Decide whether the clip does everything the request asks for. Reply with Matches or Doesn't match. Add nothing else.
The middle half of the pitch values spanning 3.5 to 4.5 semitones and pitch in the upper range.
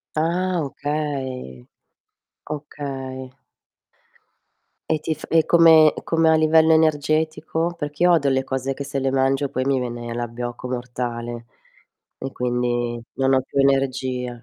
Doesn't match